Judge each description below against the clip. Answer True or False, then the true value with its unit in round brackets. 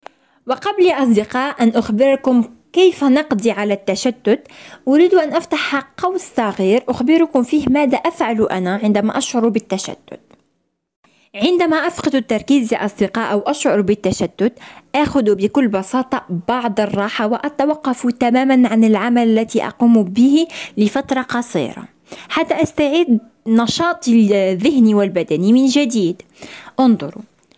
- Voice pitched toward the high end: True (245 Hz)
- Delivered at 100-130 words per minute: True (115 wpm)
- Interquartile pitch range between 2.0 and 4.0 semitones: False (4.8 semitones)